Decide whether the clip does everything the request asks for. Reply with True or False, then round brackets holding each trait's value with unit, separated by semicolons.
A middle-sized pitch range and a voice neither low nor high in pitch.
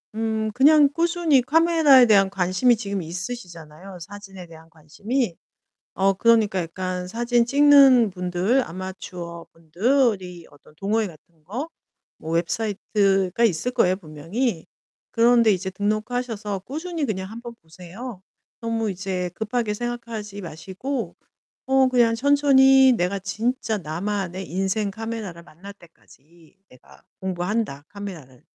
False (5.0 semitones; 205 Hz)